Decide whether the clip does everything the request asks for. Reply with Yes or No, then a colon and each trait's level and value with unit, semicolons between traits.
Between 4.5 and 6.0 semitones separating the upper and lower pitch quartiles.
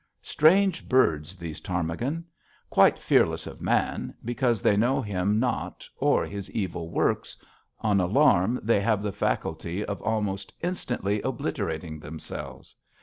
Yes: average, 5.3 semitones